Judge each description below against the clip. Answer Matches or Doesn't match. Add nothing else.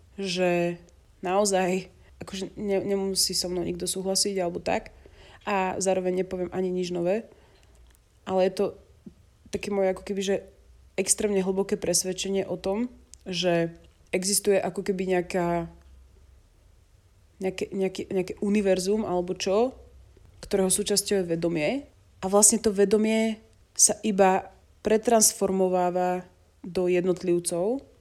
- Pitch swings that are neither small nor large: Doesn't match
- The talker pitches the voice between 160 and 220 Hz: Matches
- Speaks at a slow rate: Matches